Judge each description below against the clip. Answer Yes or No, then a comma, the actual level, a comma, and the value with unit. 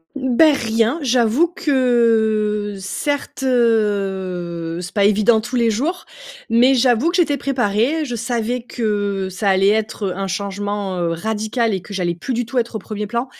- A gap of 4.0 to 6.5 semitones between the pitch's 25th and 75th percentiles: No, average, 3.5 semitones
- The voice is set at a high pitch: Yes, high, 220 Hz